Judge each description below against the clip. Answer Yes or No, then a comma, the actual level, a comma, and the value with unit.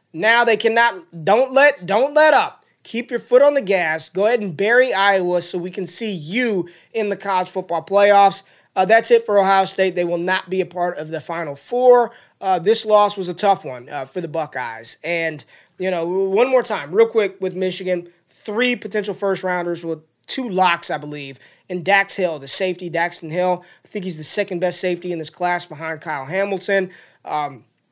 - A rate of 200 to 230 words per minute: Yes, fast, 205 wpm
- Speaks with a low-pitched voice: No, medium, 185 Hz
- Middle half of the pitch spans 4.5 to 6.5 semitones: No, average, 3.3 semitones